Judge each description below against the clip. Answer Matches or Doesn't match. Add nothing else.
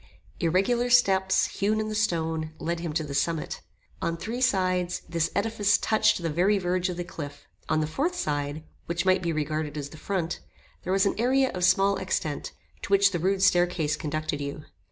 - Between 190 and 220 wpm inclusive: Matches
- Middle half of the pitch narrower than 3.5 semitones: Doesn't match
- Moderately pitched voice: Matches